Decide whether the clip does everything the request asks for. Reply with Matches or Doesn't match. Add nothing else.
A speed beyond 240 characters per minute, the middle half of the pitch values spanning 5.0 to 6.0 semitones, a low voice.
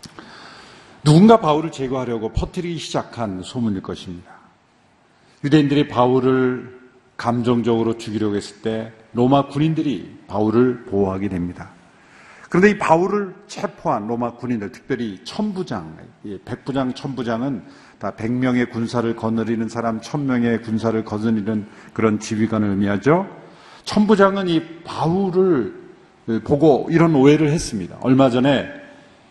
Matches